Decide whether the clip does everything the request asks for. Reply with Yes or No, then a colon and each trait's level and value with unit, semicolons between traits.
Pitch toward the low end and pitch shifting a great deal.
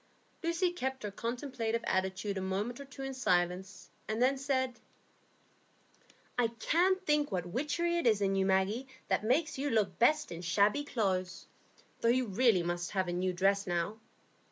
No: high, 225 Hz; wide, 6.1 semitones